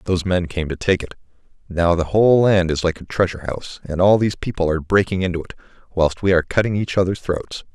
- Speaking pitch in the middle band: No, very low, 90 Hz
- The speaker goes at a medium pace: No, fast, 230 wpm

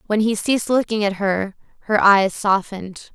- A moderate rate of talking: Yes, average, 170 wpm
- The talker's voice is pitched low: No, high, 205 Hz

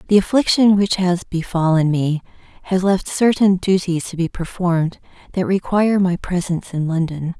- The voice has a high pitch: No, medium, 180 Hz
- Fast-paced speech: No, average, 155 wpm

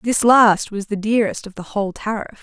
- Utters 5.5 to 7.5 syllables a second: Yes, 5.9 syllables/s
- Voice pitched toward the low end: No, high, 210 Hz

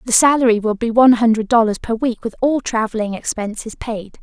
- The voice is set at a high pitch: Yes, high, 230 Hz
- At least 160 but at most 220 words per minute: Yes, average, 200 wpm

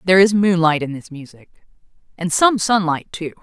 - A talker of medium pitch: Yes, medium, 175 Hz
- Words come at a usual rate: Yes, average, 175 wpm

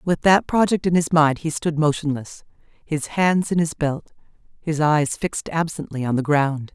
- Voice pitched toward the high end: No, medium, 155 Hz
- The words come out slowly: No, average, 180 wpm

